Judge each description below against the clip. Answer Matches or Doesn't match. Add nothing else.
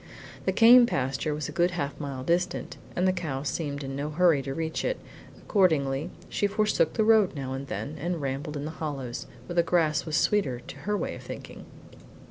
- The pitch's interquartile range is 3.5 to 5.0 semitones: Matches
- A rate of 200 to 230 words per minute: Matches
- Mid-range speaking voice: Matches